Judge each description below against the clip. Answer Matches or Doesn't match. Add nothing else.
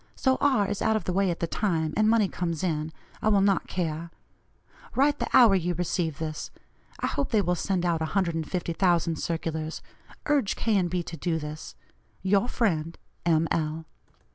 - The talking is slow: Doesn't match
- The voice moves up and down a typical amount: Matches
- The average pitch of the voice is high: Doesn't match